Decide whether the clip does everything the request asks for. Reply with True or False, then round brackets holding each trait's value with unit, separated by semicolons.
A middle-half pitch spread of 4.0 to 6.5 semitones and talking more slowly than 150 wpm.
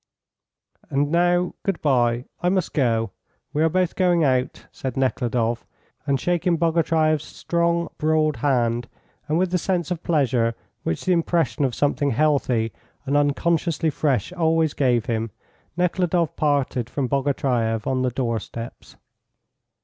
True (5.2 semitones; 140 wpm)